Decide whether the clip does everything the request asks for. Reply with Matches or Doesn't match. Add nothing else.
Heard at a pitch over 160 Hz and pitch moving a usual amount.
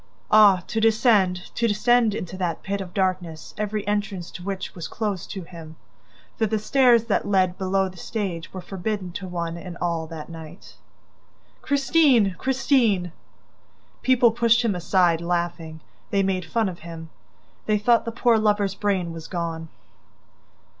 Matches